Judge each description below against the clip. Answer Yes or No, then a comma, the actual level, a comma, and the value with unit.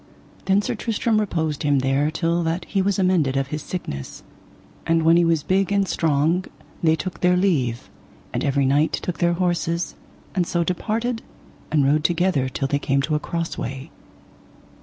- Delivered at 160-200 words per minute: Yes, average, 180 wpm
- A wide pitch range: No, average, 4.1 semitones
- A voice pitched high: No, medium, 165 Hz